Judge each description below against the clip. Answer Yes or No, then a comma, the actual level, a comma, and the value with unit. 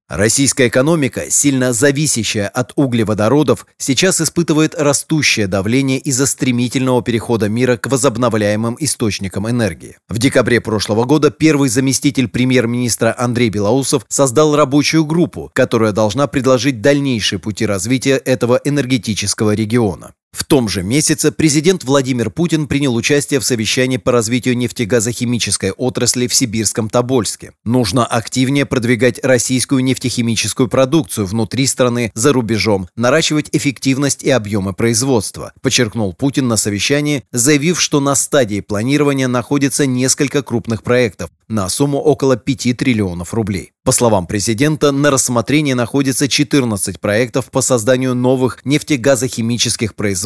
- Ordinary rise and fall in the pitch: Yes, average, 3.6 semitones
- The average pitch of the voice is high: No, low, 125 Hz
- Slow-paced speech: No, average, 125 wpm